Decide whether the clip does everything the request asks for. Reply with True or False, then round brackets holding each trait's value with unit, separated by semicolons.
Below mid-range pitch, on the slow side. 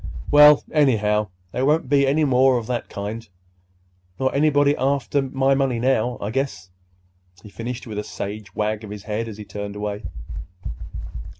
False (120 Hz; 165 wpm)